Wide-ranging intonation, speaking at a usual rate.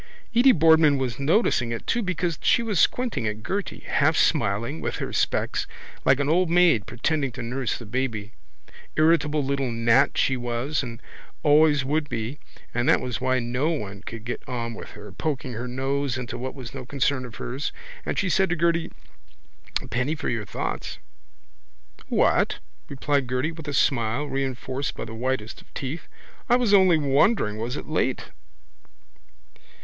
No: average, 4.7 semitones; average, 170 wpm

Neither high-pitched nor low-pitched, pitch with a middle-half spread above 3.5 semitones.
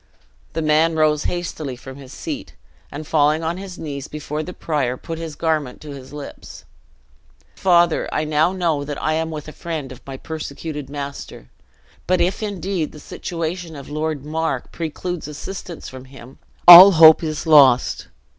No: medium, 155 Hz; narrow, 2.4 semitones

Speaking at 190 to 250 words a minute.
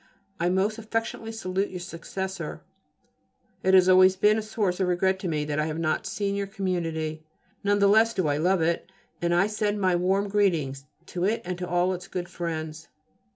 Yes: average, 200 wpm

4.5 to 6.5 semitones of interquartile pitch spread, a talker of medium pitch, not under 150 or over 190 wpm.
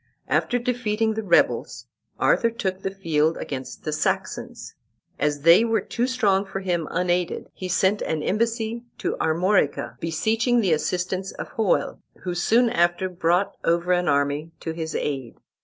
Yes: average, 5.0 semitones; medium, 180 Hz; average, 155 wpm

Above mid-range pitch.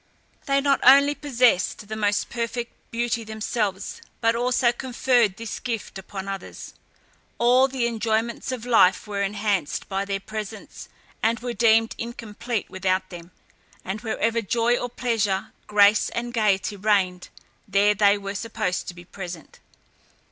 Yes: high, 220 Hz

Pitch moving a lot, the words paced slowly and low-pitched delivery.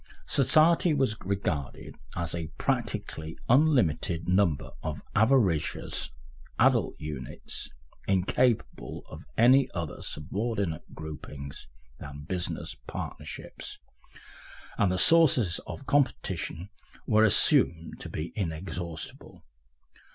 Yes: wide, 7.3 semitones; slow, 90 wpm; very low, 90 Hz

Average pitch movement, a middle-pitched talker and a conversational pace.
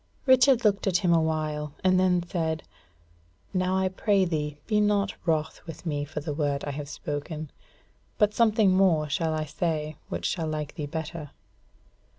Yes: average, 3.8 semitones; medium, 160 Hz; average, 170 wpm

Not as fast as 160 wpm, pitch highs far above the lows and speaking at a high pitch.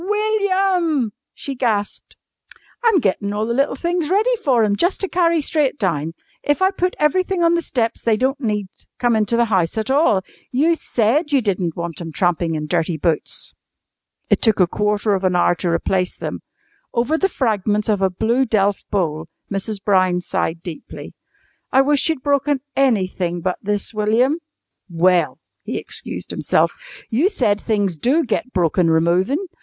No: average, 170 wpm; wide, 7.8 semitones; high, 220 Hz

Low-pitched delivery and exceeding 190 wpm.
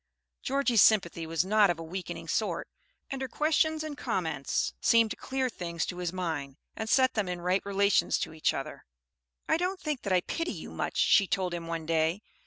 No: high, 190 Hz; average, 200 wpm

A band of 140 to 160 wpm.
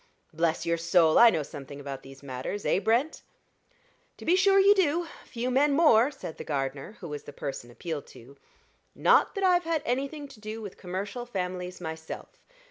No: average, 185 wpm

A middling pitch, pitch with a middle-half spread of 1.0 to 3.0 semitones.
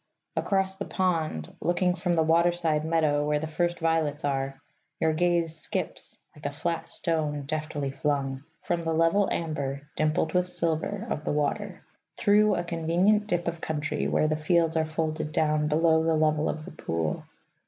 Yes: medium, 160 Hz; narrow, 2.4 semitones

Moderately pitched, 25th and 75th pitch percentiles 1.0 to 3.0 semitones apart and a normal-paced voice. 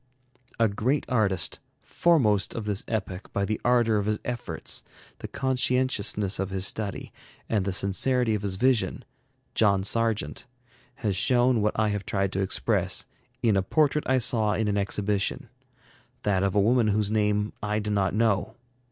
No: low, 105 Hz; average, 2.7 semitones; average, 165 wpm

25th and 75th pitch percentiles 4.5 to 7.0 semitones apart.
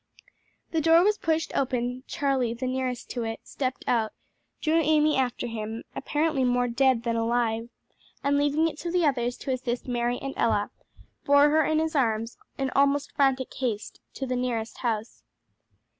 No: average, 3.4 semitones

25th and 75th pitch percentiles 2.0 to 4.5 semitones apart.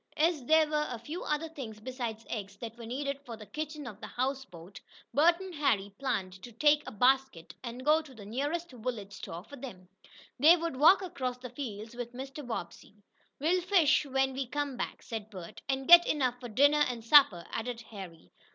No: average, 5.0 semitones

